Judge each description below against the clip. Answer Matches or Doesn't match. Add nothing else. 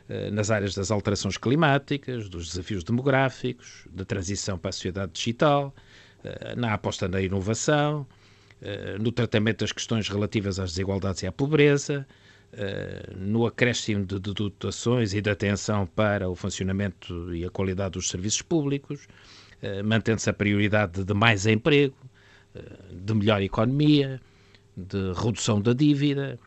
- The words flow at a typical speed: Matches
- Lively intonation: Doesn't match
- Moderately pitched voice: Doesn't match